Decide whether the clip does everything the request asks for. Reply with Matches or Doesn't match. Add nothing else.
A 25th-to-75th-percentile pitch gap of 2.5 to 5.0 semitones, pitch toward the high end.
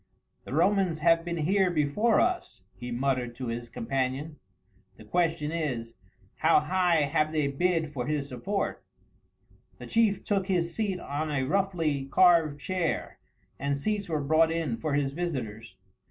Doesn't match